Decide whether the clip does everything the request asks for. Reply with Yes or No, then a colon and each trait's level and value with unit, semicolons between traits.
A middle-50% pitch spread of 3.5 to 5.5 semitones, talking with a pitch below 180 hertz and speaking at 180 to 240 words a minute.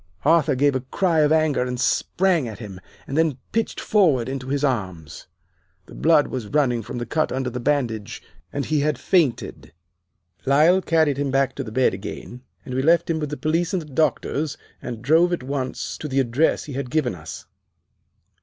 Yes: average, 3.9 semitones; medium, 140 Hz; average, 195 wpm